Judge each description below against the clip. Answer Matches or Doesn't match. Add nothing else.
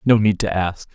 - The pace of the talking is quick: Matches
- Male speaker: Matches